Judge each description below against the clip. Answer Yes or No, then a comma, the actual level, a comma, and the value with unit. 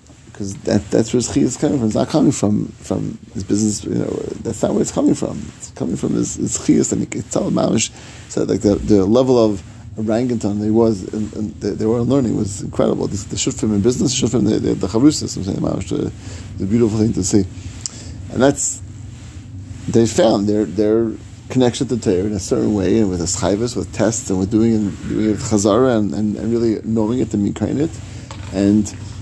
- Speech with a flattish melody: Yes, narrow, 2.0 semitones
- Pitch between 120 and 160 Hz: No, low, 105 Hz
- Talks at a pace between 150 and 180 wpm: No, average, 190 wpm